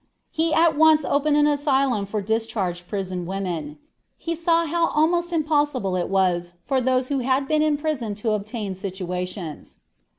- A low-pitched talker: No, very high, 255 Hz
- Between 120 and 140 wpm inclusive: No, average, 160 wpm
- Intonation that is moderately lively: No, wide, 8.0 semitones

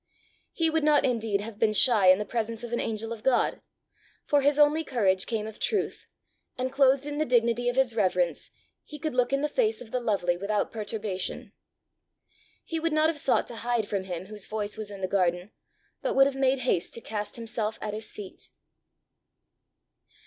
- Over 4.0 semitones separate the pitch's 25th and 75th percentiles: Yes, average, 4.6 semitones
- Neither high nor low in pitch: No, high, 230 Hz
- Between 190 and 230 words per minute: Yes, average, 200 wpm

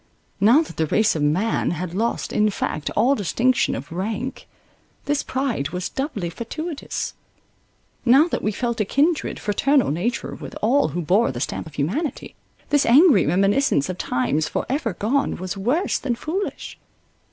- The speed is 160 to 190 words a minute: Yes, average, 165 wpm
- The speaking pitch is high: Yes, high, 220 Hz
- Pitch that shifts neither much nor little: No, wide, 7.4 semitones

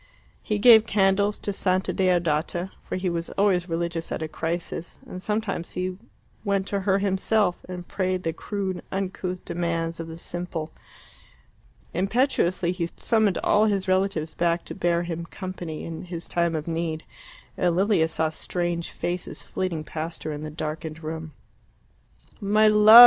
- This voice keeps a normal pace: Yes, average, 155 wpm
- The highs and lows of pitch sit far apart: No, average, 2.8 semitones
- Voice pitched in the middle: Yes, medium, 180 Hz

